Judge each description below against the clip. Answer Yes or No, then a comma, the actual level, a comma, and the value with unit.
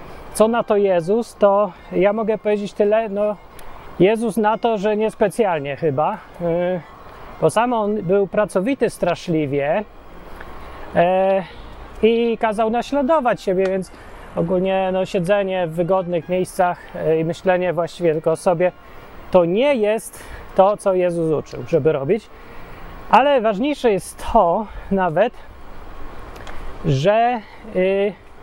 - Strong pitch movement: No, average, 3.5 semitones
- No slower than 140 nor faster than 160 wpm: No, average, 115 wpm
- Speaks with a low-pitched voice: No, high, 195 Hz